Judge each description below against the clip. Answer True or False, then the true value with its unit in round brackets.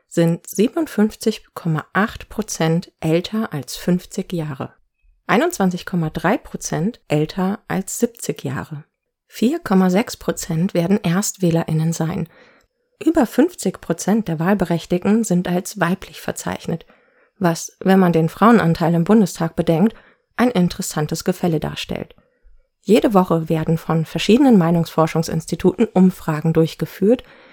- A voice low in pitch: False (180 Hz)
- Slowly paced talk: True (95 wpm)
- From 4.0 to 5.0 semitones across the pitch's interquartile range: True (4.3 semitones)